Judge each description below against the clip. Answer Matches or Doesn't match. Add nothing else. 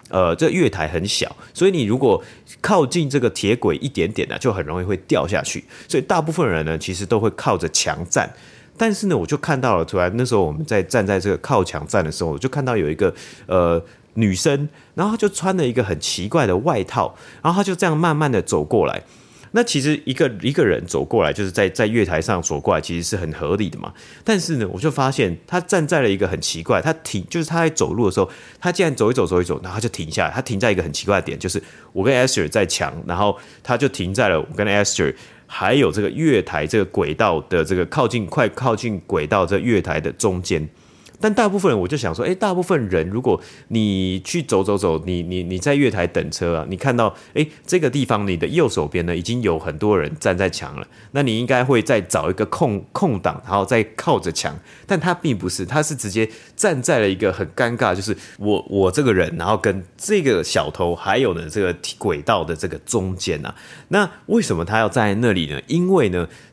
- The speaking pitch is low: Matches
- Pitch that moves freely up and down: Matches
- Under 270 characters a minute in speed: Doesn't match